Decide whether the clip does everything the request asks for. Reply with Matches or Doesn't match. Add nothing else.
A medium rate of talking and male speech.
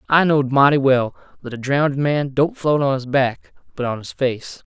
Doesn't match